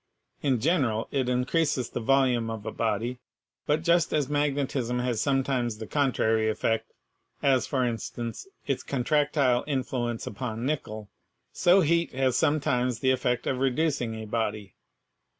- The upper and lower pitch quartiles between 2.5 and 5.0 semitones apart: Yes, average, 3.6 semitones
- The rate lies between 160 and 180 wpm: No, average, 150 wpm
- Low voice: Yes, low, 125 Hz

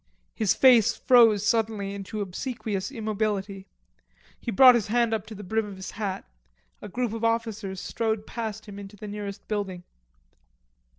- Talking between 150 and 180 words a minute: Yes, average, 160 wpm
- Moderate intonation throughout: No, narrow, 2.3 semitones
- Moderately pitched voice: No, high, 215 Hz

